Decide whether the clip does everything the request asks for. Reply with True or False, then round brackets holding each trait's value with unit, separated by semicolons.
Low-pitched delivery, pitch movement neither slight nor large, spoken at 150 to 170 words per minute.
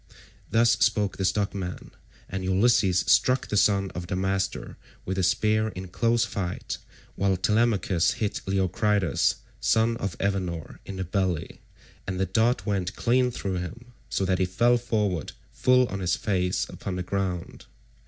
True (95 Hz; 3.2 semitones; 155 wpm)